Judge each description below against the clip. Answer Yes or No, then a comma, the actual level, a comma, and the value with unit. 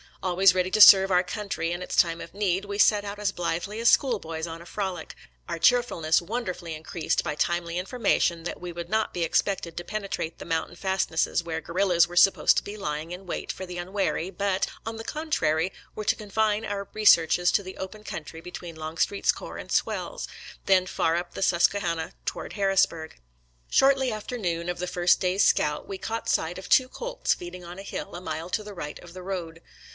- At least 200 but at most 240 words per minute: Yes, fast, 205 wpm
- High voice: No, medium, 180 Hz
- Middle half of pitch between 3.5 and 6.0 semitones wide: No, average, 3.1 semitones